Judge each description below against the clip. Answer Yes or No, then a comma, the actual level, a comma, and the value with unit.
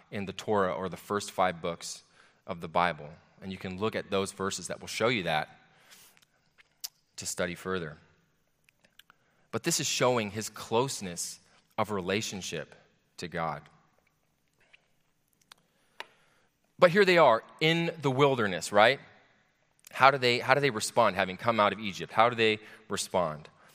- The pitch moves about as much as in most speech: No, wide, 6.1 semitones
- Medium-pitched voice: No, low, 105 Hz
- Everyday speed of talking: Yes, average, 150 wpm